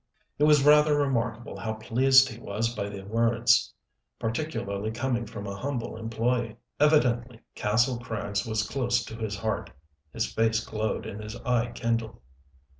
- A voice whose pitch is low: Yes, low, 115 Hz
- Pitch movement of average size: No, narrow, 2.2 semitones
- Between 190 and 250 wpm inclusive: No, average, 150 wpm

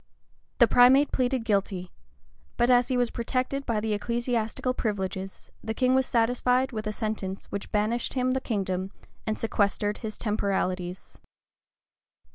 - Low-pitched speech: No, high, 225 Hz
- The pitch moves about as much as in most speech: Yes, average, 3.6 semitones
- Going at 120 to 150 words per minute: Yes, average, 140 wpm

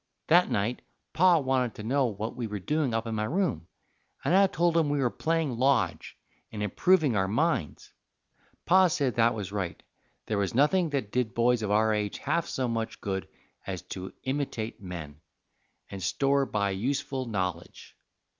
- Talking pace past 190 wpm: No, average, 175 wpm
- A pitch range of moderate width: No, wide, 5.9 semitones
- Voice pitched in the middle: No, low, 120 Hz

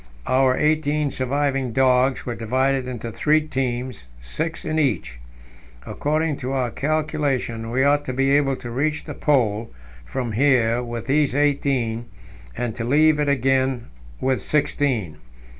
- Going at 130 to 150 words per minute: Yes, average, 140 wpm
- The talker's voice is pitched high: No, low, 130 Hz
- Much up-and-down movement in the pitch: No, average, 3.2 semitones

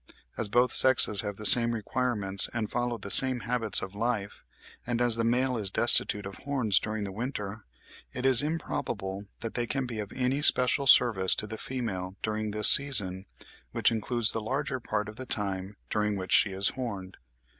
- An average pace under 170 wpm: No, average, 190 wpm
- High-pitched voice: No, low, 110 Hz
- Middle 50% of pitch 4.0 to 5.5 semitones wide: No, average, 3.5 semitones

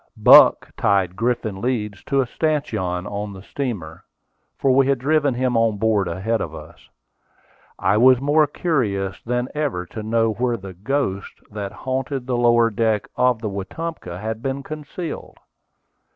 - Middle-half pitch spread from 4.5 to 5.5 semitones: Yes, average, 4.8 semitones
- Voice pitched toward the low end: Yes, low, 115 Hz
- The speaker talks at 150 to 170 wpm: Yes, average, 155 wpm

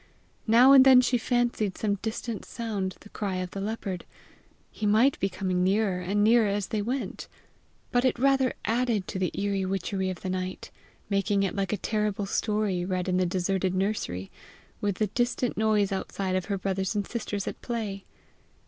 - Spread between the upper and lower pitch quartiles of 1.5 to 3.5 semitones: Yes, average, 2.9 semitones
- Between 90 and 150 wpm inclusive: No, average, 185 wpm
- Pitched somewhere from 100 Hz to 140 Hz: No, high, 205 Hz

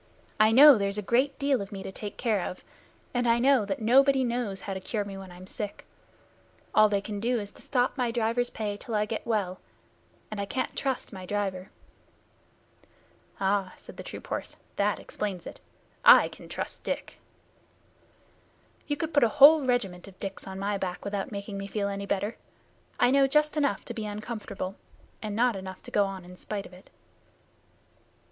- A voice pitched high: Yes, high, 210 Hz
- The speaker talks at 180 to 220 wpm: Yes, average, 195 wpm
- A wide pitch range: No, average, 3.8 semitones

